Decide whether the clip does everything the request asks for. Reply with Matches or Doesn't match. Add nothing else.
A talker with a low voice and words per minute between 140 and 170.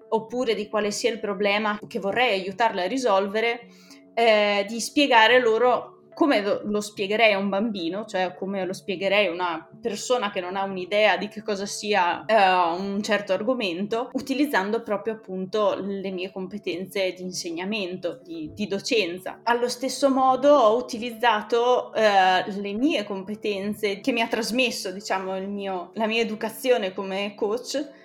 Doesn't match